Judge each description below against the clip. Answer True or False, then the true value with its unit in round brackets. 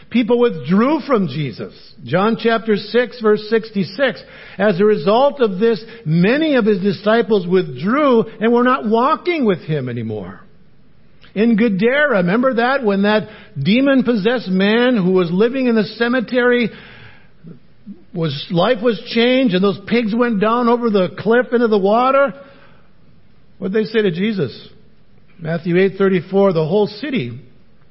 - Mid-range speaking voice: False (220 Hz)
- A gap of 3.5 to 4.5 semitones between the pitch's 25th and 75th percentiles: True (3.9 semitones)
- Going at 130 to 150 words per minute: True (140 wpm)